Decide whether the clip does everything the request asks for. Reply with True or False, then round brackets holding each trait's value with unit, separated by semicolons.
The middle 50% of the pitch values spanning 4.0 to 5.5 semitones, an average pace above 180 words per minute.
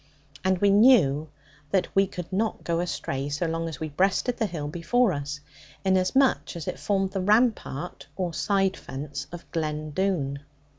False (4.5 semitones; 165 wpm)